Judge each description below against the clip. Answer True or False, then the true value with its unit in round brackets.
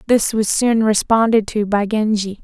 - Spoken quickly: False (175 wpm)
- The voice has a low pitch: False (215 Hz)